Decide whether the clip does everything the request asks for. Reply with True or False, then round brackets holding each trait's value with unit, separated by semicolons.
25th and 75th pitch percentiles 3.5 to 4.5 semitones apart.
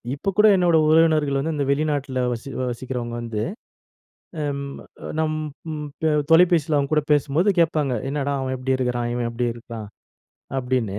True (3.9 semitones)